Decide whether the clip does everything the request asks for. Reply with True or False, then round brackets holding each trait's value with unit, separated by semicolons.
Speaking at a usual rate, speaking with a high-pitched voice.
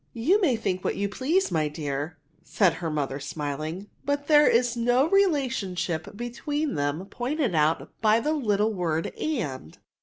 True (170 wpm; 205 Hz)